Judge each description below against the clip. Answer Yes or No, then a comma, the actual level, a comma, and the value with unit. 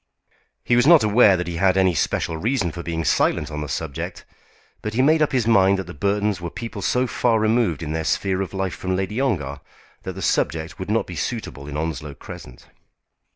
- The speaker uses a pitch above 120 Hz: No, very low, 95 Hz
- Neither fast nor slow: No, fast, 215 wpm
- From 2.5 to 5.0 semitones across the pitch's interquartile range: No, wide, 5.4 semitones